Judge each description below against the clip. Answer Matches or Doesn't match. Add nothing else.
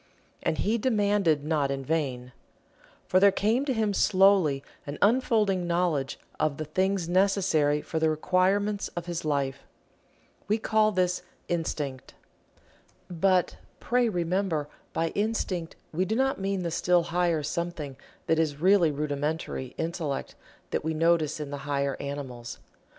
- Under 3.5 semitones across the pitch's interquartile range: Doesn't match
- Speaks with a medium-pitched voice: Matches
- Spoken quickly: Doesn't match